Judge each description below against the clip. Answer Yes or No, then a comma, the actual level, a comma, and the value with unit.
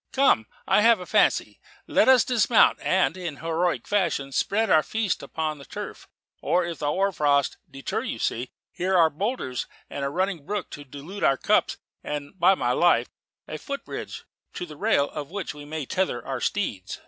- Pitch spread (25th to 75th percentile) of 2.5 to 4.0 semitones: No, wide, 5.5 semitones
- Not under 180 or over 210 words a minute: Yes, average, 190 wpm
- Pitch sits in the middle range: Yes, medium, 170 Hz